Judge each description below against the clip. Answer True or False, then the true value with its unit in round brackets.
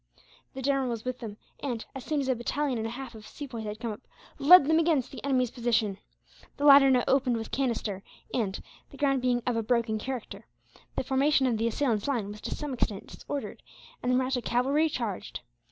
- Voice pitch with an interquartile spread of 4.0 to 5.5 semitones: False (3.3 semitones)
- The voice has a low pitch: False (250 Hz)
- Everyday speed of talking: False (210 wpm)